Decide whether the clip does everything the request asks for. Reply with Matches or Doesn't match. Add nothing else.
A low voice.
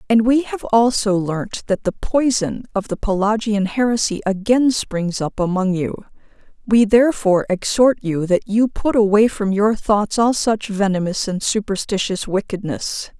Doesn't match